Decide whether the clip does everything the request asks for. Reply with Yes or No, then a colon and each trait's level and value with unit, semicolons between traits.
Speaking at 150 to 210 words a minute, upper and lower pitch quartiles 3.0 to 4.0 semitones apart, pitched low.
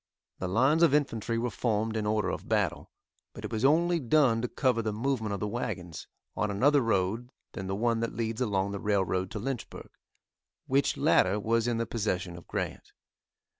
Yes: average, 190 wpm; average, 3.5 semitones; low, 115 Hz